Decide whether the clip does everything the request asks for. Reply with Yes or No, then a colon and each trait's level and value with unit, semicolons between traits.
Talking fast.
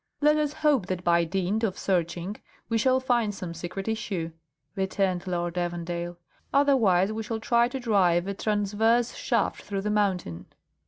No: average, 160 wpm